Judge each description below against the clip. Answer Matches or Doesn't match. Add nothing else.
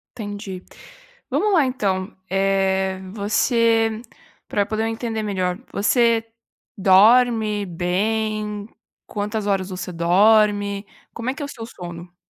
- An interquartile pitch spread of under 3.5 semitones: Matches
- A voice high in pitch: Matches